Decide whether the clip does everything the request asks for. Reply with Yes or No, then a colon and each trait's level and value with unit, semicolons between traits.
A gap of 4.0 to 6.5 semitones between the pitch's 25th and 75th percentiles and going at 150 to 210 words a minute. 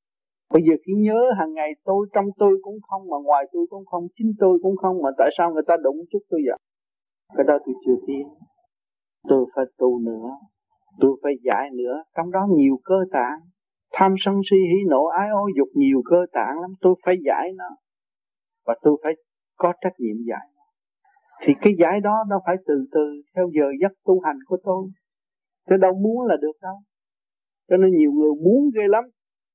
Yes: average, 5.1 semitones; average, 200 wpm